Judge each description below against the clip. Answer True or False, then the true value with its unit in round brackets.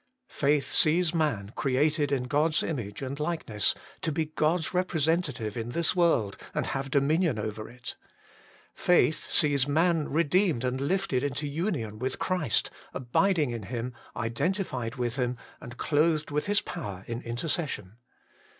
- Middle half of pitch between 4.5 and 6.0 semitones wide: True (5.1 semitones)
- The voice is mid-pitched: True (145 Hz)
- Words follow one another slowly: False (150 wpm)